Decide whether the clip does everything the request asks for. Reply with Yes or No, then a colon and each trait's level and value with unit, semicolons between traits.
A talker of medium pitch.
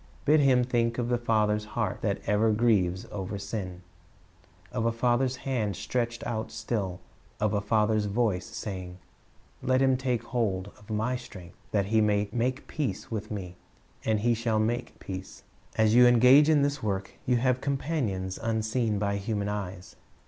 No: low, 110 Hz